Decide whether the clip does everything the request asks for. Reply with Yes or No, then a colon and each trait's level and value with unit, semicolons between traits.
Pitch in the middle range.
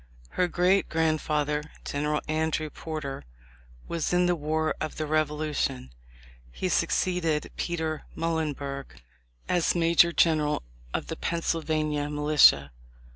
Yes: medium, 155 Hz